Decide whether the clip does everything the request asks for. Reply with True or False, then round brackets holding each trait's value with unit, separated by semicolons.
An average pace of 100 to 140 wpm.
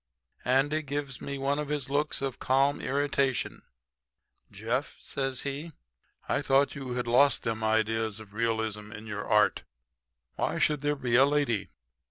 False (155 wpm)